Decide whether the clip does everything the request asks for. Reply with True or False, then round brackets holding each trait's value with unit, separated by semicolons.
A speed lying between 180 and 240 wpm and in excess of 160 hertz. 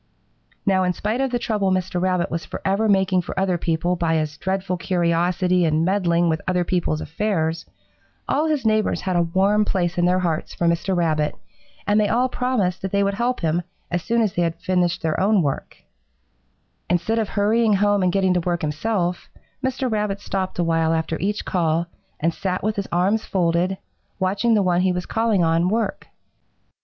True (190 wpm; 185 Hz)